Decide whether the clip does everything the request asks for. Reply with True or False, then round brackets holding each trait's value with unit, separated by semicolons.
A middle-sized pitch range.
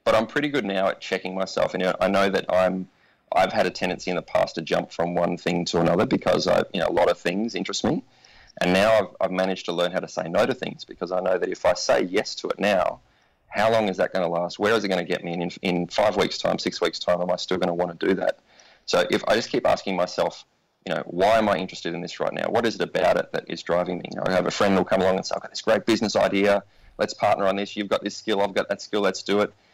False (2.1 semitones)